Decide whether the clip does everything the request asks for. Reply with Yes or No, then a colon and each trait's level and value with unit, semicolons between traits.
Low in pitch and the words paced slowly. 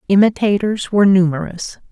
No: high, 195 Hz; slow, 95 wpm